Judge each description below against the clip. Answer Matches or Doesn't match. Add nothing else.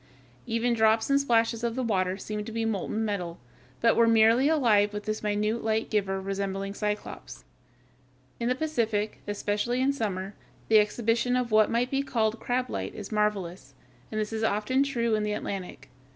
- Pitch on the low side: Doesn't match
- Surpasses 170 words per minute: Matches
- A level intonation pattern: Matches